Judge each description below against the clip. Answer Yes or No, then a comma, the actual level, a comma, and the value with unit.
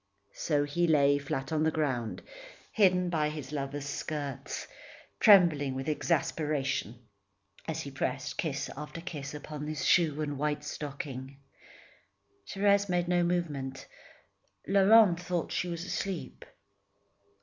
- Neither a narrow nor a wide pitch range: Yes, average, 3.7 semitones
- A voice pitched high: No, medium, 150 Hz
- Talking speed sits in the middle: No, slow, 125 wpm